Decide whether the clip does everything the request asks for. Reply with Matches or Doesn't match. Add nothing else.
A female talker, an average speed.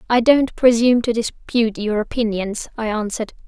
Matches